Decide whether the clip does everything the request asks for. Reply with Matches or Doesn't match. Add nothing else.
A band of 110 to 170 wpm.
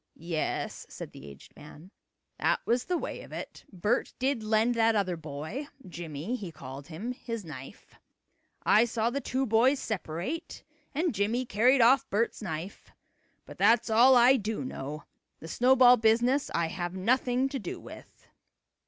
Matches